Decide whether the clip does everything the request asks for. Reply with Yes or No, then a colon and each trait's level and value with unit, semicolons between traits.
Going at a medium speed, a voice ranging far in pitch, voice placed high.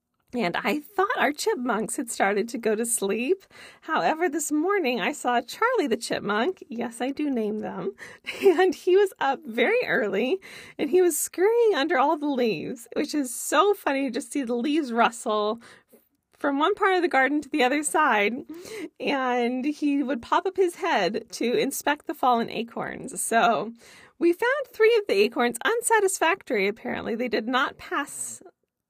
Yes: average, 170 wpm; wide, 7.3 semitones; very high, 290 Hz